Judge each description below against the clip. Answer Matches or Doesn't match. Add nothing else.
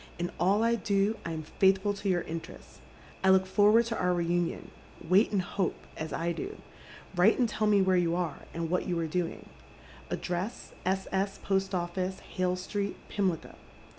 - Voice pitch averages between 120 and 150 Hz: Doesn't match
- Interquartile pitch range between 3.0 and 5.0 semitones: Doesn't match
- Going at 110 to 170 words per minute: Doesn't match